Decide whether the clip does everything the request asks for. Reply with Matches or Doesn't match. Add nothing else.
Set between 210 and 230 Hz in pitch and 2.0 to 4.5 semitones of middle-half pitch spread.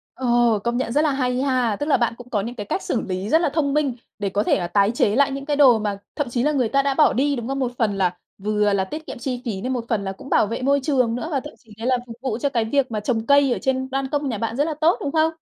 Doesn't match